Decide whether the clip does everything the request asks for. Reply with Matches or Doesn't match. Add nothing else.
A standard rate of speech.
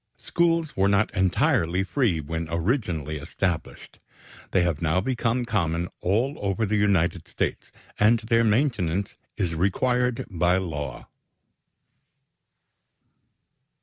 Doesn't match